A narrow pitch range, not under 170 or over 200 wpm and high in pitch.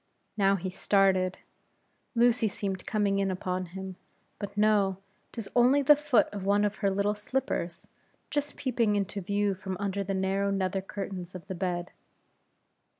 No: narrow, 1.8 semitones; average, 155 wpm; high, 195 Hz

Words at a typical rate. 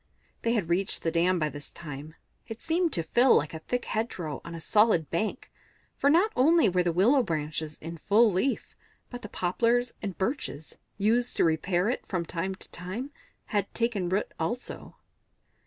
Yes: average, 180 wpm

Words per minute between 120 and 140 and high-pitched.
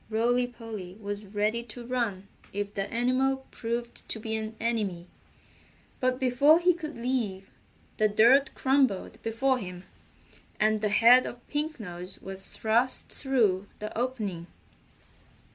Yes: slow, 135 wpm; high, 230 Hz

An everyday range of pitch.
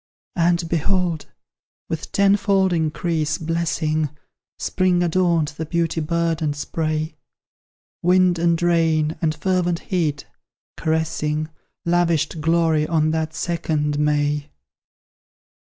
No: narrow, 1.9 semitones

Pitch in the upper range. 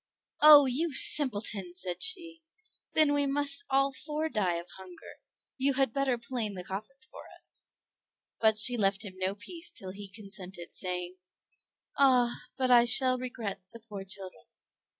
Yes: high, 235 Hz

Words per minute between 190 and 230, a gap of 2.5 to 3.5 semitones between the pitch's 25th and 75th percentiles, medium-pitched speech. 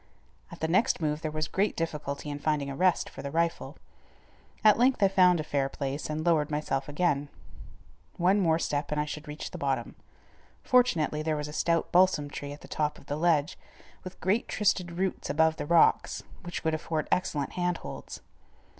Yes: average, 195 wpm; average, 3.1 semitones; medium, 155 Hz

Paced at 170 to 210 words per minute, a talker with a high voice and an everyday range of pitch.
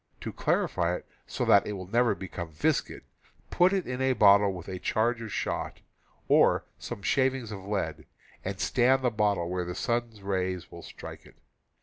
No: average, 185 wpm; low, 100 Hz; average, 4.6 semitones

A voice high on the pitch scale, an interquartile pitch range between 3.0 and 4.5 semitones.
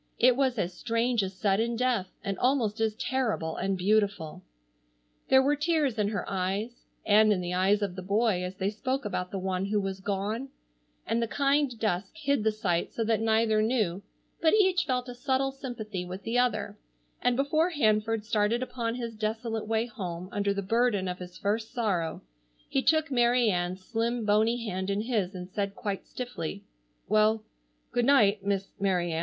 Yes: high, 215 Hz; average, 3.9 semitones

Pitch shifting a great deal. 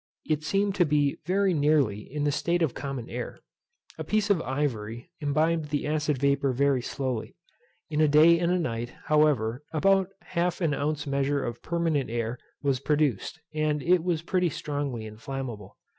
No: average, 3.5 semitones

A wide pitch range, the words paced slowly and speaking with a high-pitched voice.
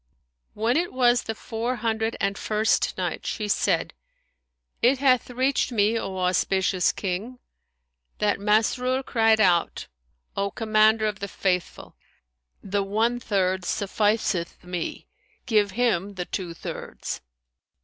No: average, 3.1 semitones; slow, 125 wpm; high, 215 Hz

